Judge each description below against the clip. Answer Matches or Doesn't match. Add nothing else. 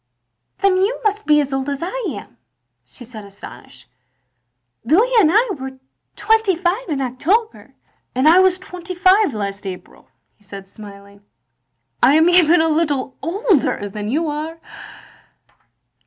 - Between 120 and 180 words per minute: Matches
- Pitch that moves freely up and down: Matches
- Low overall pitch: Doesn't match